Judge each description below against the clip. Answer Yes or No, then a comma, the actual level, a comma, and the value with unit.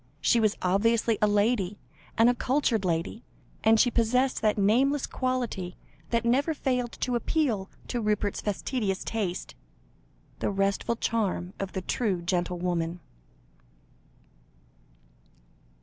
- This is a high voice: Yes, high, 220 Hz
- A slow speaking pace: Yes, slow, 120 wpm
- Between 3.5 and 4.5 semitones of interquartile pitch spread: Yes, average, 4.1 semitones